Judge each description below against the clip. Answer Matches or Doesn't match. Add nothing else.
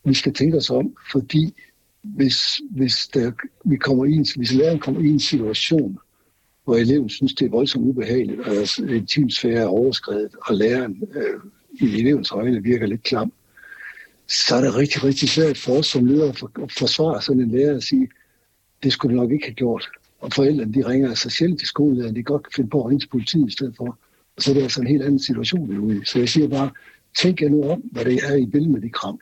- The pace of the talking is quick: Matches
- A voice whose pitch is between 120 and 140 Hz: Matches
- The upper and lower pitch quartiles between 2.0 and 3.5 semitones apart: Matches